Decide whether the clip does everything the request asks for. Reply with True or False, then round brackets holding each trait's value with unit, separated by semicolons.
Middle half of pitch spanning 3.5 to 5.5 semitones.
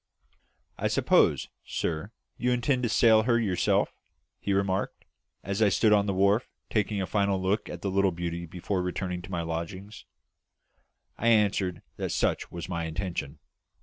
False (3.1 semitones)